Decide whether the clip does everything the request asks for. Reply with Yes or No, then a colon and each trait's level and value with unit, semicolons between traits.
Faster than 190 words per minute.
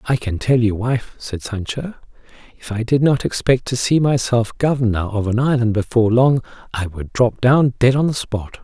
Yes: average, 200 wpm